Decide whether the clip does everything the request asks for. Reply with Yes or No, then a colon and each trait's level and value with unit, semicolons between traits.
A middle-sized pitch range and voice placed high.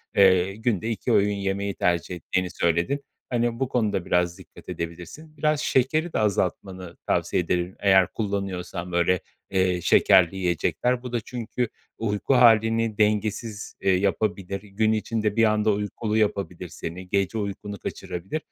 No: average, 3.5 semitones; low, 100 Hz